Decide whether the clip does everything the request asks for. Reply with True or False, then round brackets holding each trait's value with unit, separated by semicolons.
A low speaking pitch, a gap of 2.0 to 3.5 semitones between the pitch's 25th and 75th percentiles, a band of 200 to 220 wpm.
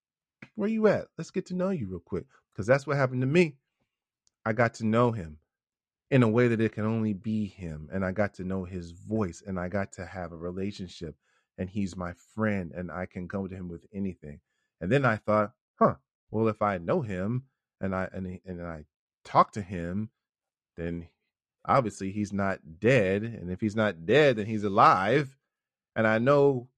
False (100 Hz; 4.1 semitones; 205 wpm)